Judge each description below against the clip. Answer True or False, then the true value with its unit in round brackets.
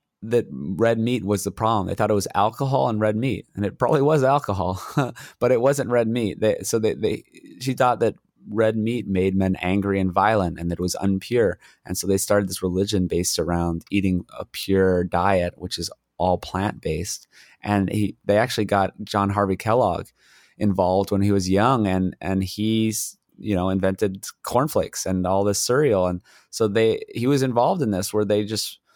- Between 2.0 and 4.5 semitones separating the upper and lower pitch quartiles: True (2.8 semitones)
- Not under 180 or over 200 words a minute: True (195 wpm)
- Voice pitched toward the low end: True (100 Hz)